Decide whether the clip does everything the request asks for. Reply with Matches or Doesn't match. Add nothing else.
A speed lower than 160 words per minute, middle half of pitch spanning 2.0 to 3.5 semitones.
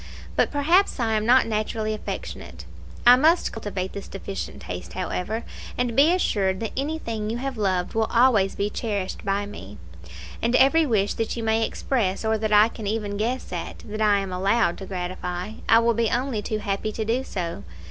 Doesn't match